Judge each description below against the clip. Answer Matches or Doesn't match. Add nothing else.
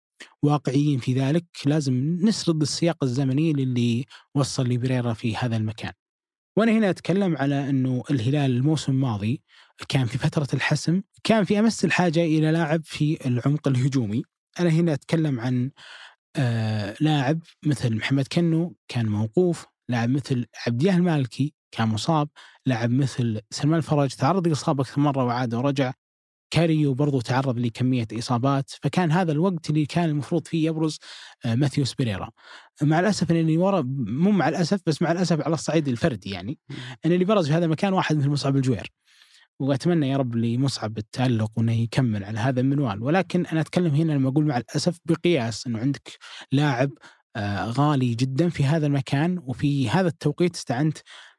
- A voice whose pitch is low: Doesn't match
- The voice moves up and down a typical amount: Matches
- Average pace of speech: Doesn't match